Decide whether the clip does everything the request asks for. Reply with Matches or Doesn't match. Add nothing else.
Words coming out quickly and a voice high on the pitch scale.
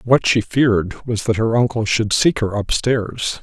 Doesn't match